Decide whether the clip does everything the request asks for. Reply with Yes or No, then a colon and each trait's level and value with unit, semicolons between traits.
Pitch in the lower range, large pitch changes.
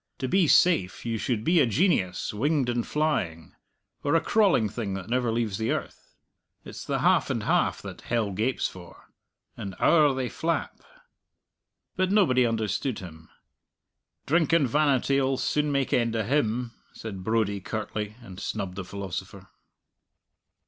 Yes: low, 115 Hz; wide, 6.1 semitones